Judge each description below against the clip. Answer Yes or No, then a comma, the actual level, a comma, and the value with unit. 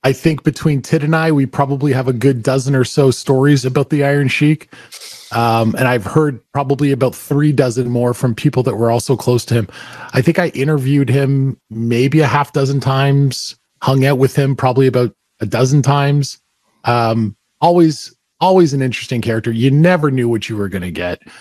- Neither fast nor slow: Yes, average, 195 wpm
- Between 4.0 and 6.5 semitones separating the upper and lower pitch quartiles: No, average, 2.9 semitones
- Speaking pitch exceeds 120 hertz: Yes, low, 135 Hz